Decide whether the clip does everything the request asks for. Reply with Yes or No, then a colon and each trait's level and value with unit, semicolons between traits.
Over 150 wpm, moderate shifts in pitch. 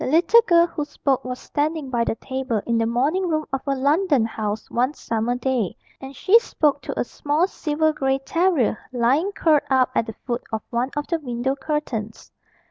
Yes: average, 200 wpm; average, 4.4 semitones